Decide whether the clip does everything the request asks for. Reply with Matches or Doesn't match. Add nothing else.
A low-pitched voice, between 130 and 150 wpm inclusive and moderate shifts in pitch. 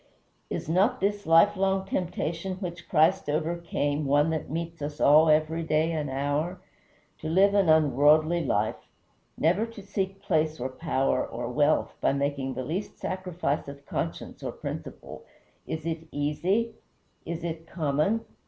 Doesn't match